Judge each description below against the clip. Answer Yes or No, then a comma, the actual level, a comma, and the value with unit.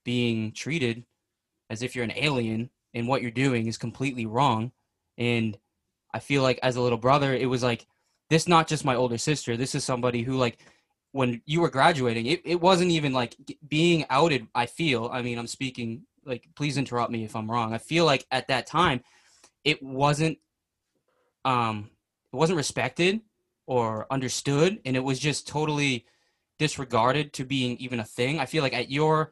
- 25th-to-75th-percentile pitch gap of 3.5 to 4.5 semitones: Yes, average, 3.8 semitones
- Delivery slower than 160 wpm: No, average, 185 wpm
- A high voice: No, low, 130 Hz